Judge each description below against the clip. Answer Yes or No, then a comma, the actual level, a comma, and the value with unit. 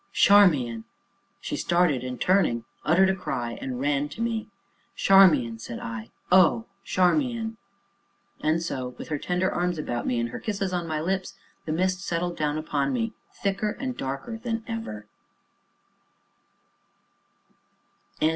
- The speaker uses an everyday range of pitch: No, wide, 6.5 semitones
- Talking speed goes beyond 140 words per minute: No, slow, 135 wpm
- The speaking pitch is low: No, medium, 175 Hz